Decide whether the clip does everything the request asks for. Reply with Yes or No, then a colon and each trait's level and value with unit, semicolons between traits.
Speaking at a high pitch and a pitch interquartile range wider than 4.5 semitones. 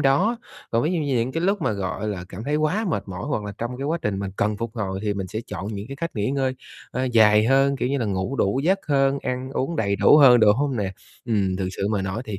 No: low, 120 Hz; wide, 5.4 semitones